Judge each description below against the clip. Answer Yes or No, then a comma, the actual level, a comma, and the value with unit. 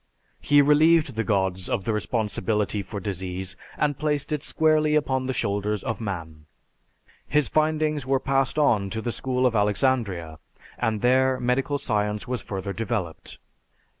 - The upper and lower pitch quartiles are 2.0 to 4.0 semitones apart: No, wide, 5.6 semitones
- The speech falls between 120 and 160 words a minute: Yes, average, 150 wpm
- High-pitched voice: No, low, 120 Hz